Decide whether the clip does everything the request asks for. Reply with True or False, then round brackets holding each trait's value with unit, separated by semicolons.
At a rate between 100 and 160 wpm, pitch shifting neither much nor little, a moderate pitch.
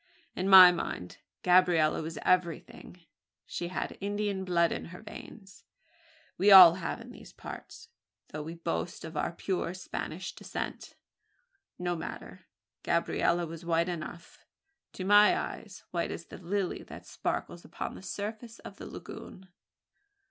False (140 wpm; 2.2 semitones; 180 Hz)